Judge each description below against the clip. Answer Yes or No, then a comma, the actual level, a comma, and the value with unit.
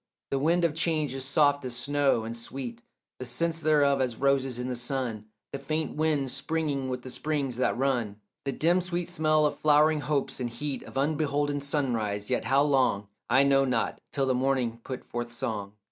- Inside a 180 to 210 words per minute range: Yes, average, 190 wpm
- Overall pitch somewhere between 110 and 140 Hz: Yes, low, 135 Hz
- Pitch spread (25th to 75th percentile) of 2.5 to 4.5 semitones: Yes, average, 3.1 semitones